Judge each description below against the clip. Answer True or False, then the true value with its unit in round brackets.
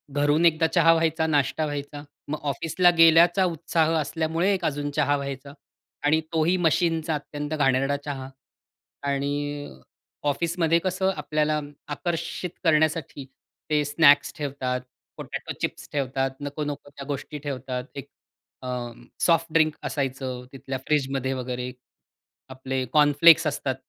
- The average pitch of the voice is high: False (145 Hz)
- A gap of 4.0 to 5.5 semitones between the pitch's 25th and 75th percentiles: False (2.9 semitones)